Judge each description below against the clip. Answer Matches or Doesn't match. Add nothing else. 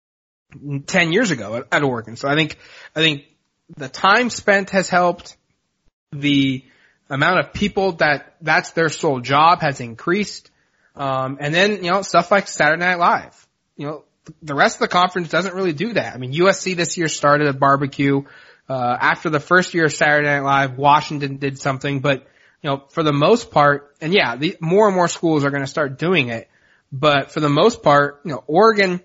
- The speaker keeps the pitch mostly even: Doesn't match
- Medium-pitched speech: Matches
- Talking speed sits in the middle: Matches